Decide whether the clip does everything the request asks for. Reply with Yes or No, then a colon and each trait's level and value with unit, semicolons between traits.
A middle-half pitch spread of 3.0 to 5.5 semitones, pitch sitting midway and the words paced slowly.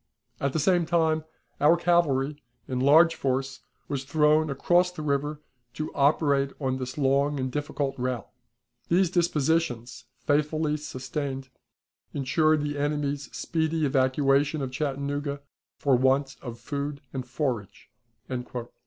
No: narrow, 2.5 semitones; medium, 145 Hz; slow, 125 wpm